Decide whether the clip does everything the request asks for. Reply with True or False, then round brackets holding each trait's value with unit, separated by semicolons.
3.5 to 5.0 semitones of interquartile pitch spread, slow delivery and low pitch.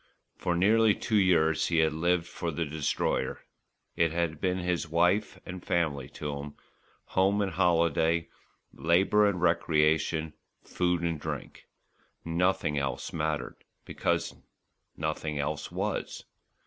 False (2.4 semitones; 120 wpm; 85 Hz)